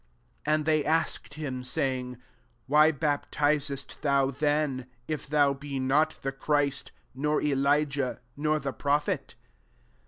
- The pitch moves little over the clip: Yes, narrow, 1.9 semitones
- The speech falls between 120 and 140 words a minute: Yes, slow, 135 wpm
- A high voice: No, medium, 145 Hz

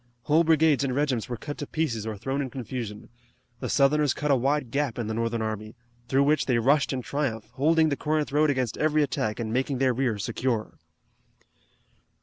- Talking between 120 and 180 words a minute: No, average, 195 wpm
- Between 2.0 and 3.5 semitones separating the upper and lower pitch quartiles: No, average, 4.2 semitones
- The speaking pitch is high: No, low, 135 Hz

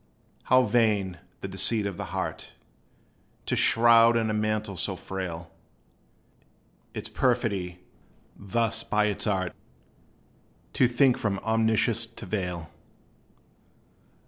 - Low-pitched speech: Yes, low, 105 Hz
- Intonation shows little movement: No, average, 3.3 semitones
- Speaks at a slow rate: Yes, slow, 110 wpm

